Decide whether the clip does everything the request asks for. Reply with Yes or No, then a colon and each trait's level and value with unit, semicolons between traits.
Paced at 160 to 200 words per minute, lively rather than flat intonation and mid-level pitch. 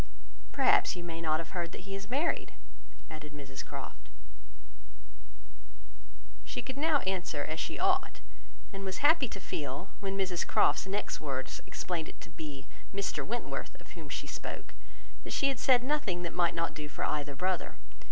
Yes: average, 170 wpm; wide, 6.5 semitones; medium, 180 Hz